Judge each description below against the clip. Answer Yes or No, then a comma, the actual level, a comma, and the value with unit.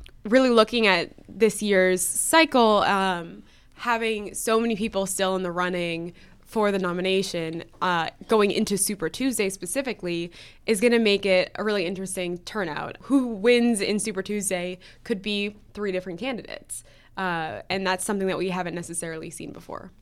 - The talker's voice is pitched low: No, high, 195 Hz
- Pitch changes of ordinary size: Yes, average, 3.4 semitones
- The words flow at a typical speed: Yes, average, 160 wpm